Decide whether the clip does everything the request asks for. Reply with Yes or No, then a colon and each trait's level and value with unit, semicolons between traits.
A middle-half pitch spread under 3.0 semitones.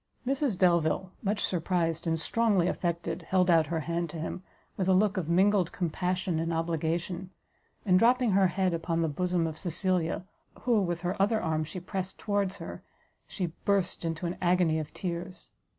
Yes: narrow, 2.4 semitones